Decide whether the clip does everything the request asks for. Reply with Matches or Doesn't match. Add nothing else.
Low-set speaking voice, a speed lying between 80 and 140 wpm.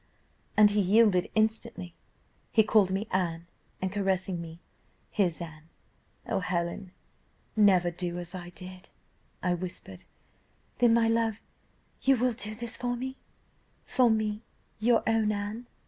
Doesn't match